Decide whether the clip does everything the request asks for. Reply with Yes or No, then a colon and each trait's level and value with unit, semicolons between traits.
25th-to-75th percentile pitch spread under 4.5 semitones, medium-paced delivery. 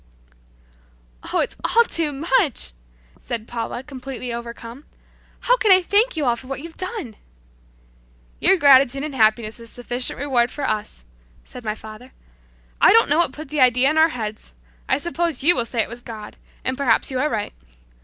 No: average, 4.8 semitones; average, 185 wpm